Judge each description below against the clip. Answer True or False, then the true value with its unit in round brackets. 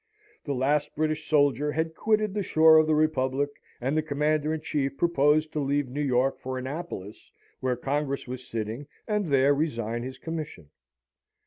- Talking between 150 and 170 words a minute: True (165 wpm)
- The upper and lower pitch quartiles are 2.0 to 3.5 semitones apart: True (3.0 semitones)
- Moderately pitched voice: True (145 Hz)